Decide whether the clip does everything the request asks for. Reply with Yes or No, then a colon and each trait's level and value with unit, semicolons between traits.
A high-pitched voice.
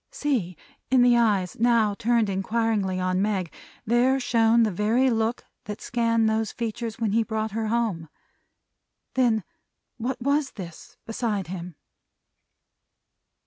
Yes: high, 225 Hz